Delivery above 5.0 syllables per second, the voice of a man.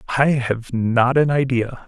No: 4.0 syllables/s; male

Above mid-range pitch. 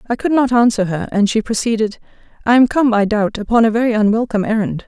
Yes: high, 220 Hz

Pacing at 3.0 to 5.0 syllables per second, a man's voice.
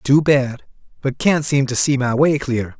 Yes: 4.2 syllables/s; male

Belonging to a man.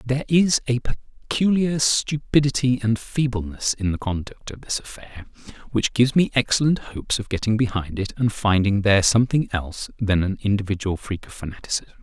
Yes: male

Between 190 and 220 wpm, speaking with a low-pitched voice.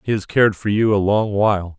No: fast, 270 wpm; low, 100 Hz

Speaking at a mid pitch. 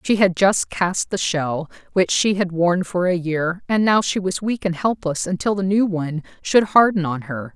Yes: medium, 175 Hz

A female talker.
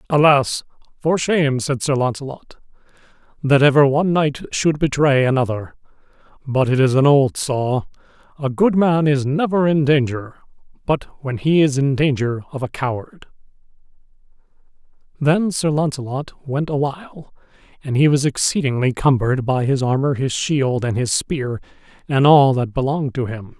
No: male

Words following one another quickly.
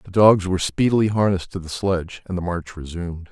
Yes: fast, 215 wpm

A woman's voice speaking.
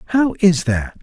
No: male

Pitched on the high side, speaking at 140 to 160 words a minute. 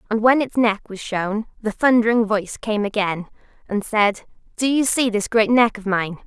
No: high, 215 Hz; average, 200 wpm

